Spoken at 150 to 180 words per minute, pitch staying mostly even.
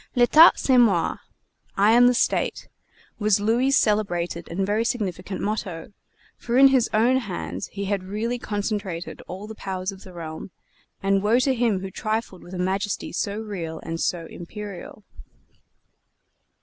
No: average, 155 wpm; average, 3.6 semitones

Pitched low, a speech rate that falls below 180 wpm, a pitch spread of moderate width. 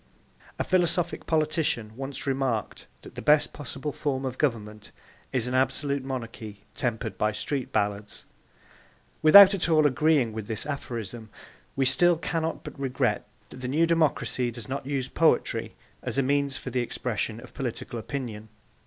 Yes: low, 130 Hz; average, 155 wpm; average, 4.1 semitones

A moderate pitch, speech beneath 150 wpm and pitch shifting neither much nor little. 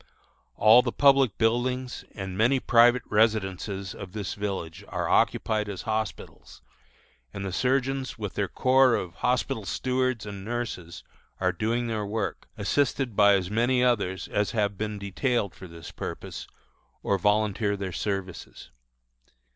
No: low, 105 Hz; average, 140 wpm; average, 3.8 semitones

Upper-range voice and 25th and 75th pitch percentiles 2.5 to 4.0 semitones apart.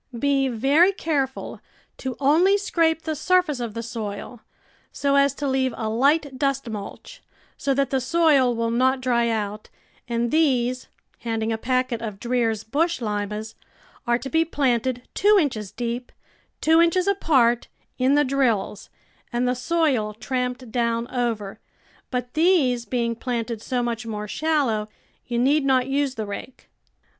Yes: very high, 250 Hz; average, 3.6 semitones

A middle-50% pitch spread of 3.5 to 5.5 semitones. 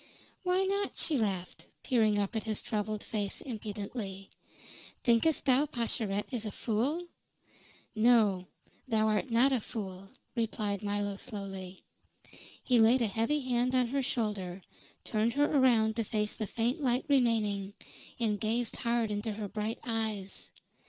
No: average, 3.1 semitones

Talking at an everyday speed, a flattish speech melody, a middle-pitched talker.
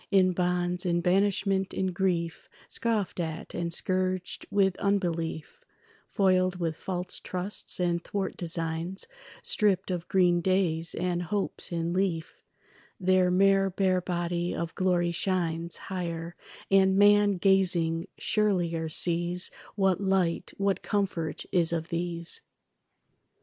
No: slow, 120 wpm; narrow, 2.1 semitones; medium, 180 Hz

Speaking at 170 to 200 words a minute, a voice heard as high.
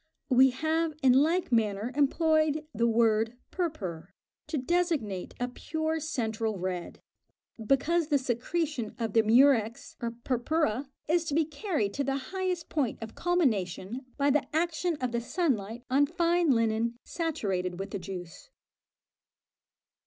No: average, 140 wpm; very high, 260 Hz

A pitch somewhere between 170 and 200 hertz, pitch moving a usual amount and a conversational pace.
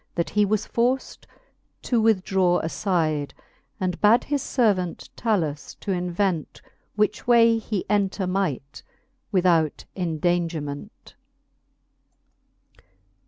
No: medium, 185 Hz; average, 3.9 semitones; slow, 95 wpm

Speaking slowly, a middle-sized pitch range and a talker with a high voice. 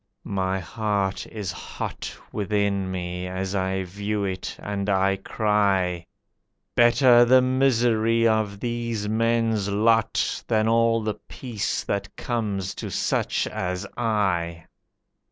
No: slow, 120 wpm; average, 3.1 semitones; low, 105 Hz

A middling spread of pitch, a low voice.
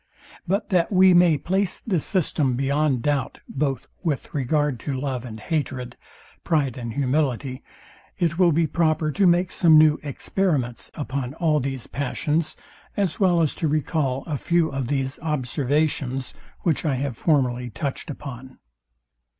No: average, 3.9 semitones; medium, 145 Hz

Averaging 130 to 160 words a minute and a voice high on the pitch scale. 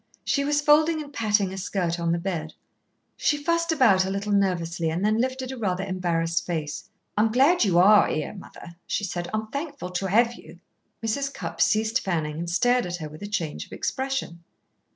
No: average, 195 wpm; high, 200 Hz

